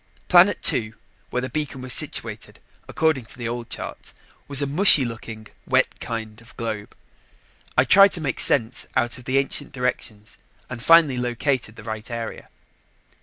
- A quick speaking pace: No, average, 165 wpm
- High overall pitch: No, low, 125 Hz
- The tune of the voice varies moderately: Yes, average, 3.7 semitones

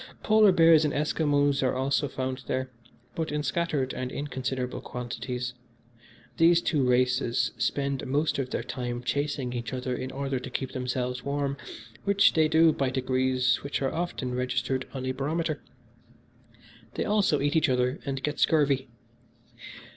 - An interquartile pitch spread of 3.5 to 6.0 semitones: No, average, 2.7 semitones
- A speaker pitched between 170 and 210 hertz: No, low, 135 Hz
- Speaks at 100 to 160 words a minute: Yes, average, 155 wpm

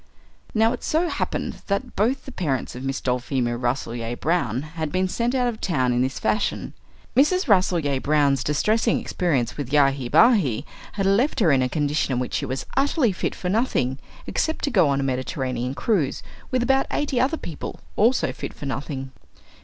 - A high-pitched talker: No, medium, 155 Hz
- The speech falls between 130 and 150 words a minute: No, average, 185 wpm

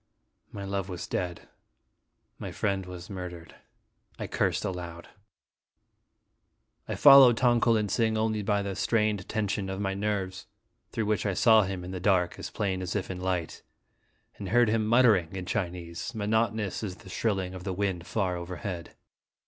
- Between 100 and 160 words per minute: No, average, 170 wpm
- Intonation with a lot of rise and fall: No, average, 2.9 semitones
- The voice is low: Yes, very low, 95 Hz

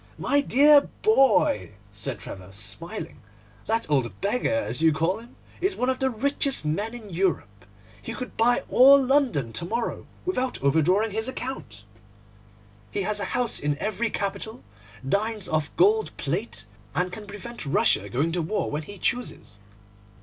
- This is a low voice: No, high, 215 Hz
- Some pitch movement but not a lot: No, wide, 8.3 semitones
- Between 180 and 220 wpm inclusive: No, average, 155 wpm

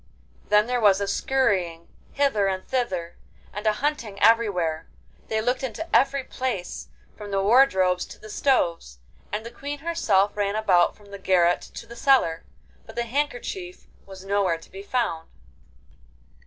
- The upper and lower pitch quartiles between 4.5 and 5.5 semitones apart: Yes, average, 4.9 semitones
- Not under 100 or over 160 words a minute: Yes, average, 155 wpm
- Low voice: No, high, 210 Hz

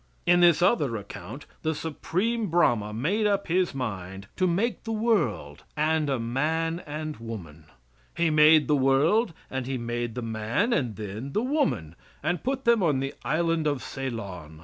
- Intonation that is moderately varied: No, wide, 7.3 semitones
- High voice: No, medium, 150 Hz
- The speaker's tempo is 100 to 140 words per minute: No, average, 170 wpm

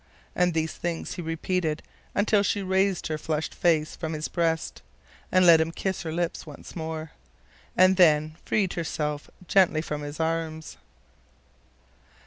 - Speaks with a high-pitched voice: No, medium, 165 Hz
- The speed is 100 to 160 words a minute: Yes, average, 145 wpm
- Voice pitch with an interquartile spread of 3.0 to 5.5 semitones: No, narrow, 2.4 semitones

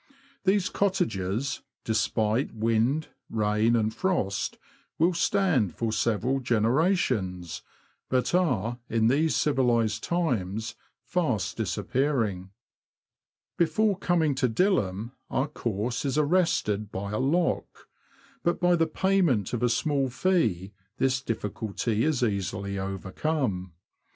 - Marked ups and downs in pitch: Yes, wide, 7.0 semitones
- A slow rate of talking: Yes, slow, 110 wpm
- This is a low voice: Yes, low, 120 Hz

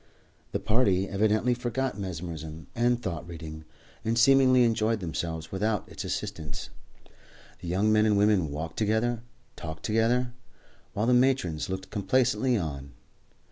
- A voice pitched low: Yes, low, 105 Hz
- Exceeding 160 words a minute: No, average, 140 wpm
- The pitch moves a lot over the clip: Yes, wide, 6.2 semitones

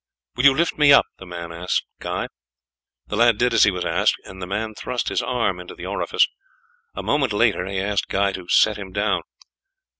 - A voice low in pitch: Yes, low, 100 Hz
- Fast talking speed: Yes, fast, 215 wpm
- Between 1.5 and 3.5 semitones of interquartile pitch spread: No, average, 4.1 semitones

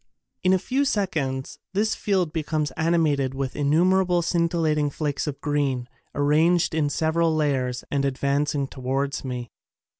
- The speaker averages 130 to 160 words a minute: Yes, average, 140 wpm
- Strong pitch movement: No, average, 3.3 semitones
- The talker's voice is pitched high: No, medium, 150 Hz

